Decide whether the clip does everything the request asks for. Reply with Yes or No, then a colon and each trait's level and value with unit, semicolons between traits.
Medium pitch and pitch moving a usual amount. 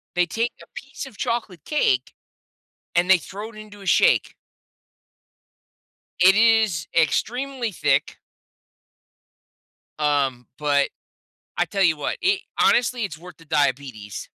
No: medium, 180 Hz; wide, 7.5 semitones